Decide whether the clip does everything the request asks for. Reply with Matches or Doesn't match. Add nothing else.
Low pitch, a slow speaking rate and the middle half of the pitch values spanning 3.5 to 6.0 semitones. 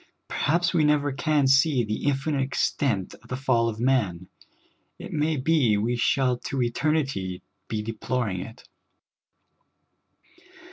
Matches